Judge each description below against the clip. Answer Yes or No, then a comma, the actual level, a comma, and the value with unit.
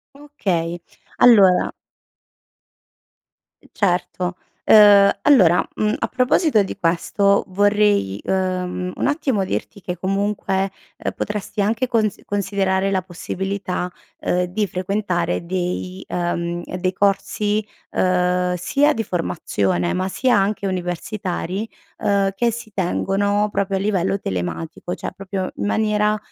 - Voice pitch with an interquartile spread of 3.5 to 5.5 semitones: No, narrow, 2.6 semitones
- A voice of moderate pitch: No, high, 195 Hz